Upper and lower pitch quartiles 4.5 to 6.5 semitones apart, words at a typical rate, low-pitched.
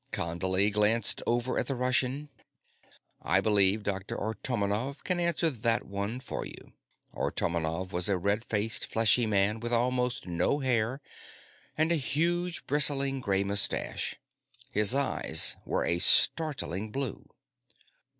No: average, 5.1 semitones; slow, 130 wpm; low, 115 Hz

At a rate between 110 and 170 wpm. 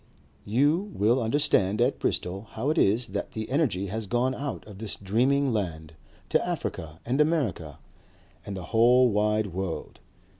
Yes: average, 155 wpm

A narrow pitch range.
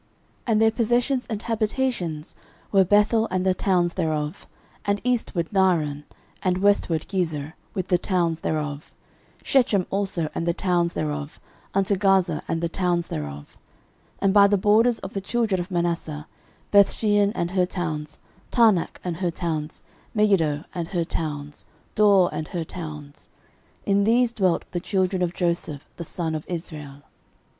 No: average, 4.0 semitones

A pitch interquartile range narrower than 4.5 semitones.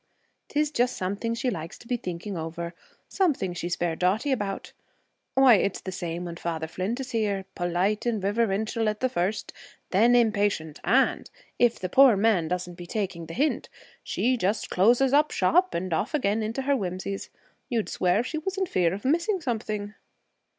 No: wide, 5.4 semitones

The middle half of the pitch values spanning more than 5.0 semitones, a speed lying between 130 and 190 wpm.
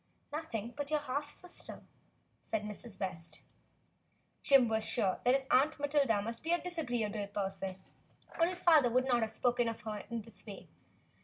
Yes: wide, 5.4 semitones; average, 175 wpm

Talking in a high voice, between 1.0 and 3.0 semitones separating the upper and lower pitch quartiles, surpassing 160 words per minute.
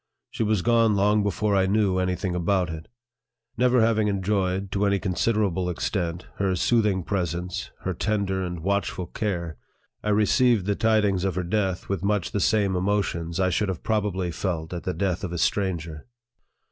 No: very low, 95 Hz; average, 2.7 semitones; average, 180 wpm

